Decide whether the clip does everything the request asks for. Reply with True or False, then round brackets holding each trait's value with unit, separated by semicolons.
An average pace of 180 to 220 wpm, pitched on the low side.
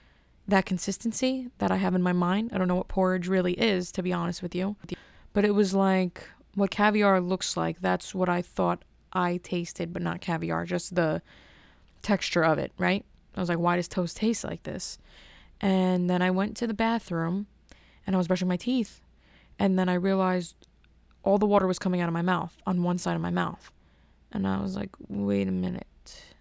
False (205 wpm; 180 Hz)